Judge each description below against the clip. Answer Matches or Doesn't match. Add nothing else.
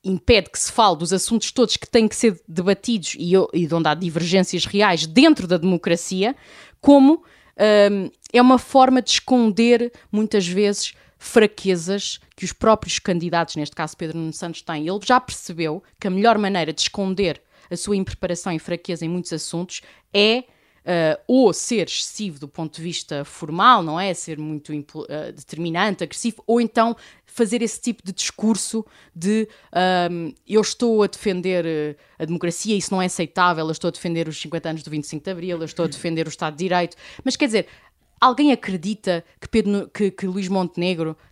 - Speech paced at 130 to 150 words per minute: Doesn't match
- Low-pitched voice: Doesn't match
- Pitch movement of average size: Matches